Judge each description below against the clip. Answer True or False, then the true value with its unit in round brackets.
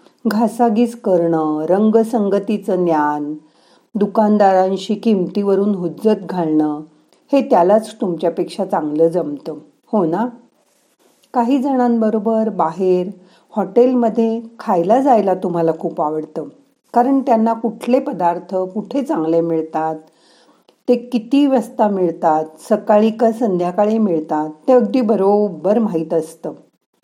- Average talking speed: True (100 wpm)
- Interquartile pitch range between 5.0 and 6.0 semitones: True (5.5 semitones)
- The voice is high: True (205 Hz)